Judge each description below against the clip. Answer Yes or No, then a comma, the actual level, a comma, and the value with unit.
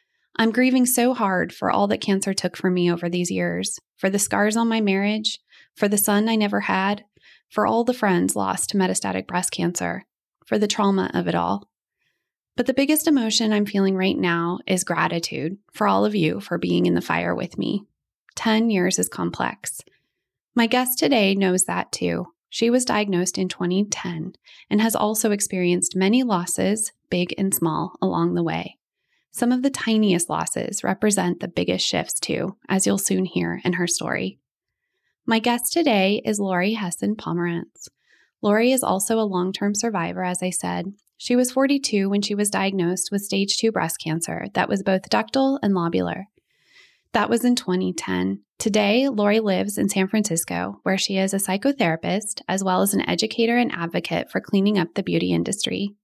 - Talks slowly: No, average, 180 wpm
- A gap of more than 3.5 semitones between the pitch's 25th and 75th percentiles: Yes, average, 4.1 semitones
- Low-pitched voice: No, high, 195 Hz